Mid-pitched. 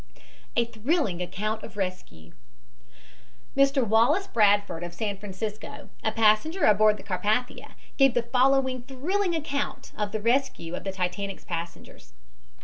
No: high, 220 Hz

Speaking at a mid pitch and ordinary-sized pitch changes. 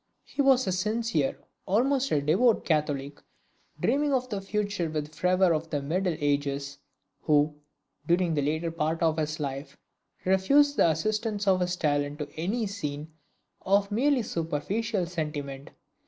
No: medium, 170 Hz; wide, 5.8 semitones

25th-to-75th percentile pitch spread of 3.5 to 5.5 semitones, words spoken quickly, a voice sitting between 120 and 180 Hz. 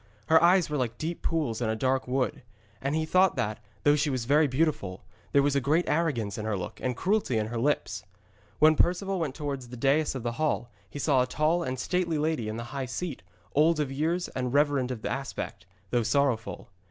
Yes: average, 4.3 semitones; fast, 215 wpm; medium, 140 Hz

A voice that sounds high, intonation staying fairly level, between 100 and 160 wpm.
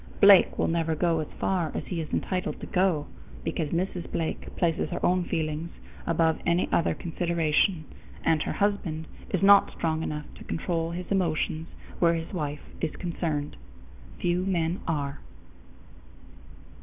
No: medium, 165 Hz; narrow, 2.1 semitones; average, 150 wpm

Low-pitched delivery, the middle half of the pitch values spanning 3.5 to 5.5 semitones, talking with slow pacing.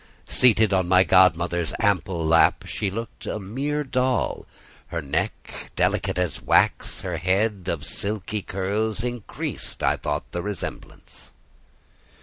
Yes: very low, 95 Hz; average, 4.1 semitones; slow, 130 wpm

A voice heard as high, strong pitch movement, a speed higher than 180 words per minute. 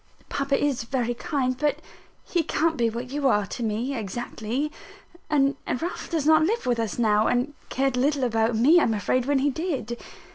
No: very high, 255 Hz; average, 3.8 semitones; average, 190 wpm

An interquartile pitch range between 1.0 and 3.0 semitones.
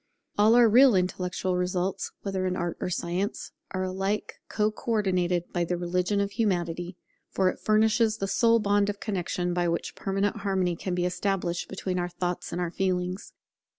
Yes: narrow, 2.4 semitones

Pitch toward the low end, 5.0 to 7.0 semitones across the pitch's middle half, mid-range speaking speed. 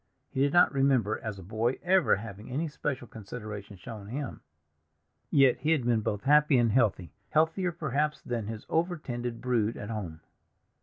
Yes: low, 120 Hz; wide, 5.4 semitones; average, 170 wpm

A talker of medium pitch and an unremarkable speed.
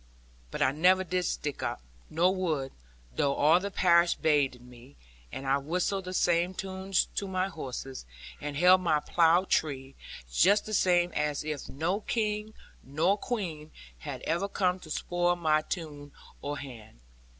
Yes: medium, 170 Hz; average, 160 wpm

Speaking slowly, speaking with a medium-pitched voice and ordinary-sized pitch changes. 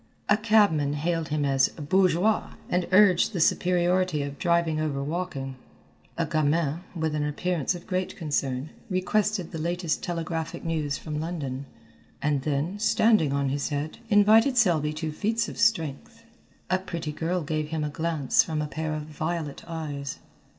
No: average, 155 wpm; medium, 160 Hz; average, 3.5 semitones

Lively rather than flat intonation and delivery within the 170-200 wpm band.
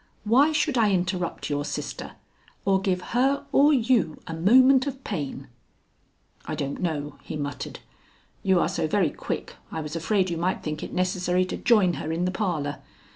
Yes: wide, 5.9 semitones; average, 180 wpm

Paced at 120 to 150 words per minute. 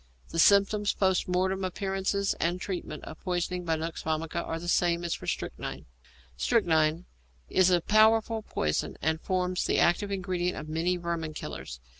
No: average, 160 wpm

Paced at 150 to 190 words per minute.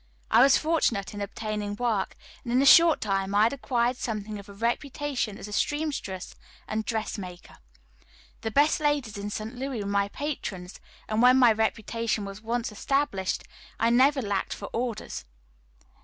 Yes: average, 170 wpm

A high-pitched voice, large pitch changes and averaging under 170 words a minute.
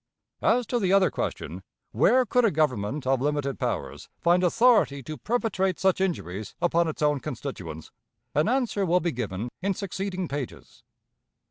No: medium, 170 Hz; wide, 6.3 semitones; average, 155 wpm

